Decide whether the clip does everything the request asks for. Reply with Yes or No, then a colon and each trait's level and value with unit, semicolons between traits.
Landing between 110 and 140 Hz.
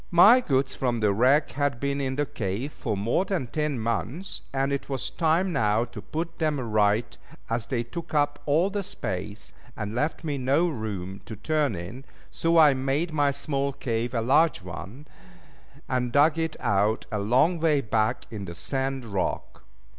Yes: low, 135 Hz